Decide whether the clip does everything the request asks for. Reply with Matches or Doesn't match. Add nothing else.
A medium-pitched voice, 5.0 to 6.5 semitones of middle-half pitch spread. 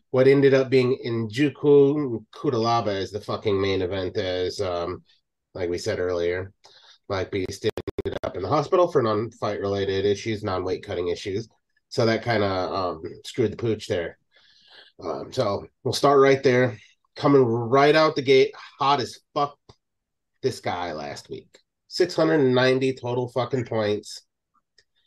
Doesn't match